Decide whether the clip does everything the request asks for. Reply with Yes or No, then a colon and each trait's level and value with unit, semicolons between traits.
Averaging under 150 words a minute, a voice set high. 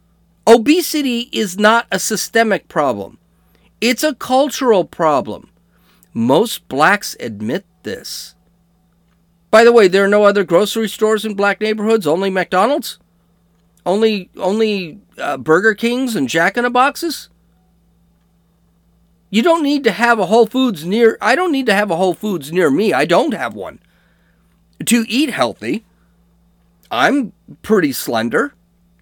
Yes: average, 140 wpm; high, 200 Hz